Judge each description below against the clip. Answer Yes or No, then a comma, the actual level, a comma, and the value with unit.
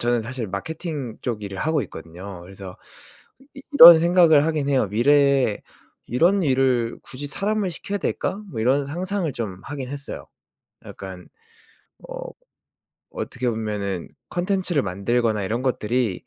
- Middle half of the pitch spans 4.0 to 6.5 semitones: No, wide, 7.0 semitones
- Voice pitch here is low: Yes, low, 130 Hz